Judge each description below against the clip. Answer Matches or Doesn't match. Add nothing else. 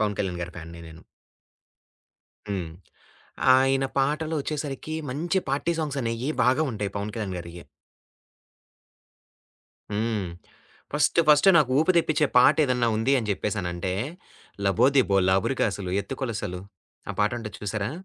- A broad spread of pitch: Matches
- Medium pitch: Doesn't match